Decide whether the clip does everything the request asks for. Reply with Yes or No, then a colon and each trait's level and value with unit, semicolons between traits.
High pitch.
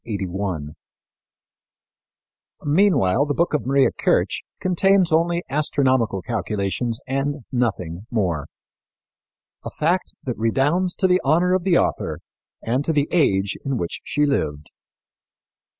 No: low, 135 Hz